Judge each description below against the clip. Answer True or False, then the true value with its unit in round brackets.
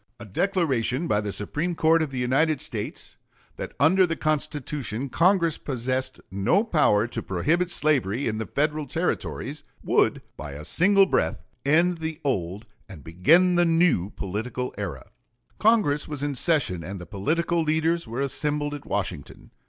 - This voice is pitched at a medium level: True (145 Hz)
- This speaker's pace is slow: False (155 wpm)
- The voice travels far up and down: True (7.1 semitones)